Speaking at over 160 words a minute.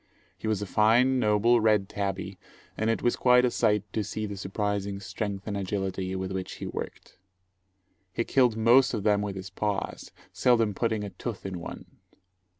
Yes: average, 180 wpm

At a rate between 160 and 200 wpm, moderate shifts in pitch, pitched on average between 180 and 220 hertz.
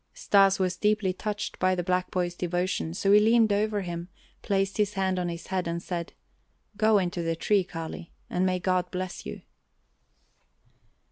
No: average, 175 wpm; narrow, 2.2 semitones; medium, 185 Hz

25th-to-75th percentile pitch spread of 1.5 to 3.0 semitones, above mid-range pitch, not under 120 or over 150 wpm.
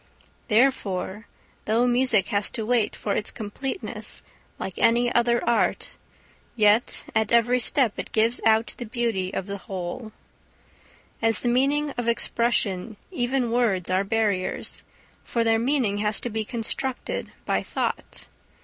Yes: narrow, 2.6 semitones; high, 225 Hz; average, 140 wpm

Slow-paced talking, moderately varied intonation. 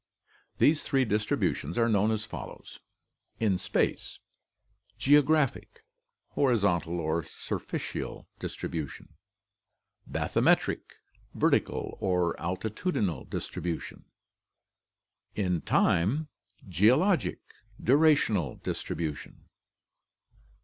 No: slow, 70 wpm; wide, 7.8 semitones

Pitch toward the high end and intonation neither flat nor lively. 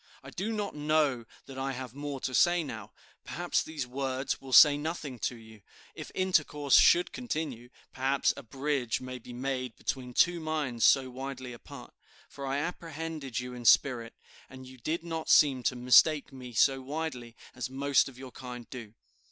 No: low, 135 Hz; average, 3.4 semitones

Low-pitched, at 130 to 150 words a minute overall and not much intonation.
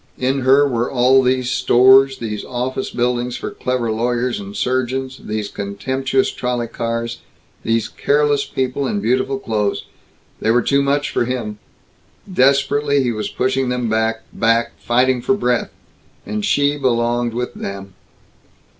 Yes: low, 125 Hz; average, 145 wpm; narrow, 2.3 semitones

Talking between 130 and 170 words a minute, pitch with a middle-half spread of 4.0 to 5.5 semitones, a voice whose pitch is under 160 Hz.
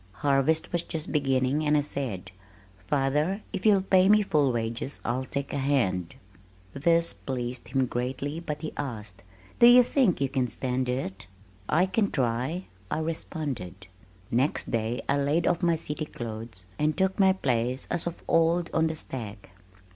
Yes: average, 165 wpm; average, 5.0 semitones; medium, 140 Hz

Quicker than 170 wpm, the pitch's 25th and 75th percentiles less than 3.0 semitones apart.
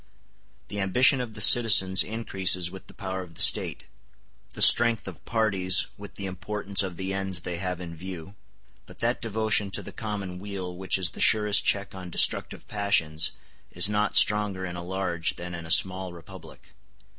Yes: average, 180 wpm; narrow, 2.5 semitones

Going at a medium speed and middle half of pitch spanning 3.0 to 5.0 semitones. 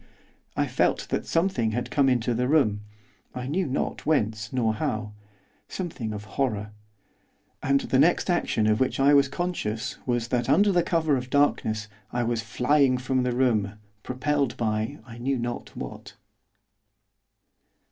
Yes: average, 155 wpm; average, 4.2 semitones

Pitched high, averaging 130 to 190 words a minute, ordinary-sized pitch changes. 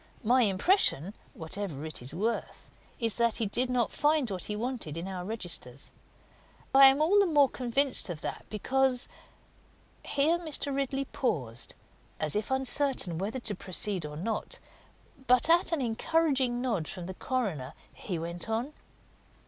No: high, 230 Hz; average, 155 wpm; wide, 6.9 semitones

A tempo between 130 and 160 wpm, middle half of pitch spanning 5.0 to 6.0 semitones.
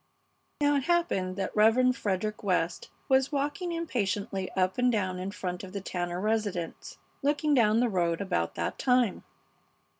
Yes: average, 155 wpm; wide, 5.5 semitones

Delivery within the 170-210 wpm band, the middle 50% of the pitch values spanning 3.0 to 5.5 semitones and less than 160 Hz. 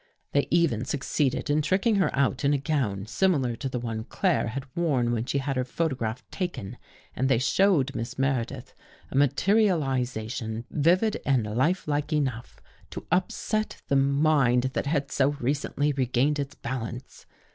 No: average, 155 wpm; average, 3.6 semitones; low, 135 Hz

